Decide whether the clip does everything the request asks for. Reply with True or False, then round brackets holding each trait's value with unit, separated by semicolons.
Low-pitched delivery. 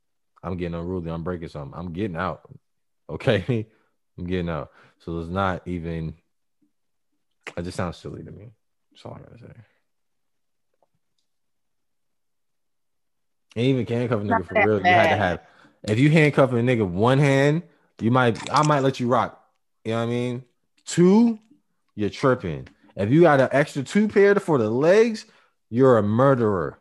True (115 Hz)